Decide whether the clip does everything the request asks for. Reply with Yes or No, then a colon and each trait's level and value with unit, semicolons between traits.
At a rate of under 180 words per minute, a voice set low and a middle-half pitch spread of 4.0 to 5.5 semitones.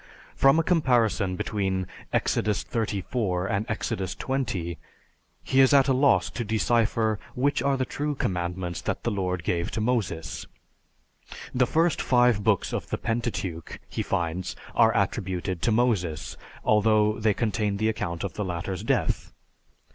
Yes: average, 145 wpm; low, 105 Hz; average, 4.7 semitones